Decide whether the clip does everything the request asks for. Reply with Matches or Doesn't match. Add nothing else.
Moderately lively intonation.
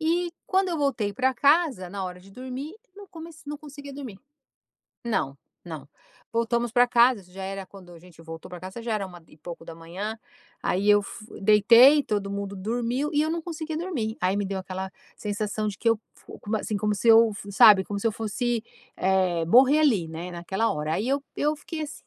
Doesn't match